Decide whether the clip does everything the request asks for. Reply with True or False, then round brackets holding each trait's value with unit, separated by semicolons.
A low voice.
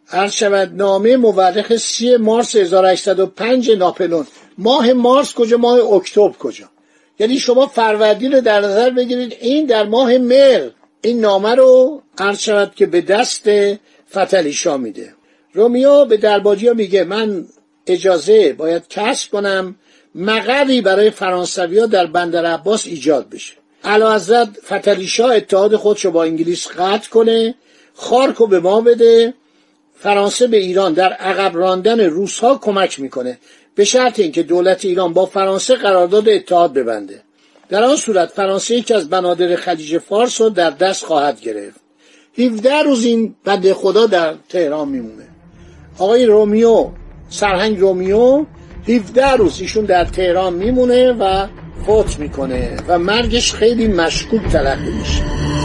False (205 Hz)